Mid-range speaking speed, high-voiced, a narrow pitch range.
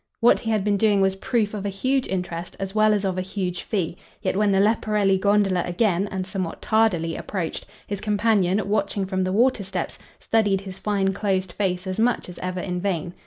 No: fast, 210 wpm; high, 195 Hz; narrow, 2.2 semitones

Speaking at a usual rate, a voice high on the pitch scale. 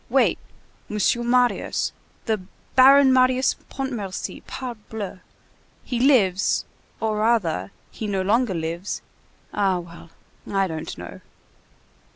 No: slow, 90 wpm; high, 215 Hz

